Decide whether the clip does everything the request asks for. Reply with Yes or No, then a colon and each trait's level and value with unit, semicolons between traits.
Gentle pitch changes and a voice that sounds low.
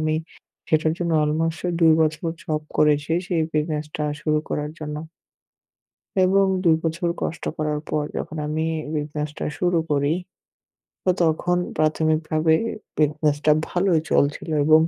No: narrow, 1.3 semitones; medium, 155 Hz